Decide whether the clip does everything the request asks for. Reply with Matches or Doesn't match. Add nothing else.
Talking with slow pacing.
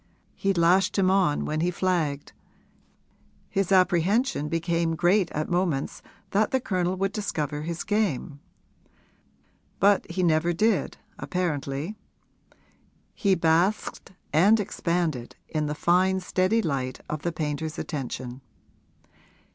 Matches